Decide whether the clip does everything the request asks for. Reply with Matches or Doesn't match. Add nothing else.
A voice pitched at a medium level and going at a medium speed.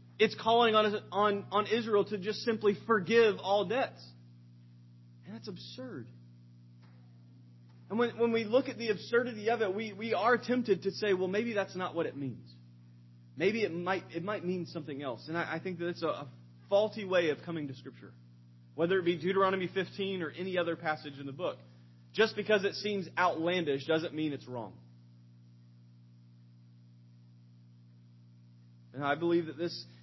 Matches